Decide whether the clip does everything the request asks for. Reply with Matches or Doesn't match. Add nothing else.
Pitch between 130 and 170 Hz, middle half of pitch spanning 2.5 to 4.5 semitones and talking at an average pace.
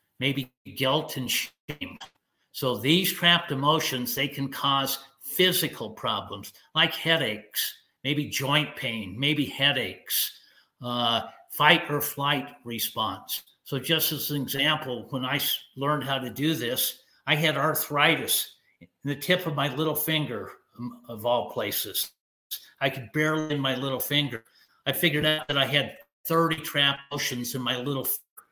Matches